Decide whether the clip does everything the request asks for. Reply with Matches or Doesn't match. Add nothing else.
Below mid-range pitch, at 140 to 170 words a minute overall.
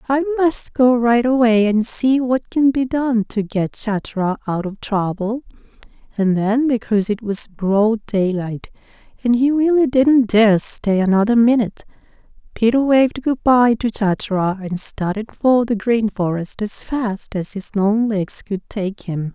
Doesn't match